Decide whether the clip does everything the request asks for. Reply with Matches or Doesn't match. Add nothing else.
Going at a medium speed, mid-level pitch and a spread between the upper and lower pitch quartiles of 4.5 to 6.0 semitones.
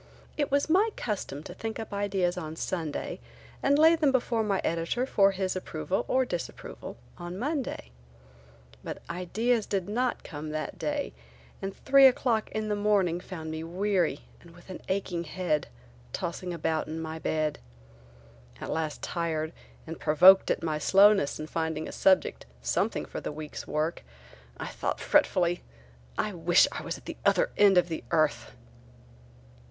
Matches